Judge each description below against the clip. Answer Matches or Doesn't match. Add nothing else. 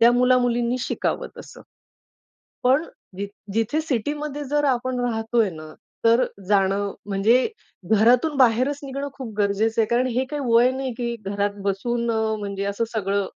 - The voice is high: Matches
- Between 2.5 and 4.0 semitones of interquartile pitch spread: Matches